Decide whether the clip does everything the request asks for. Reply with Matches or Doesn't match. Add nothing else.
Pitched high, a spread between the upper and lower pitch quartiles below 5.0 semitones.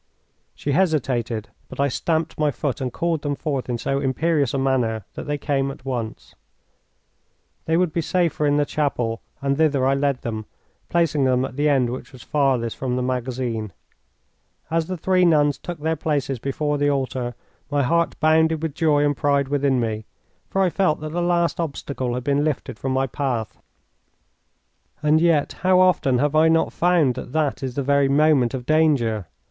Doesn't match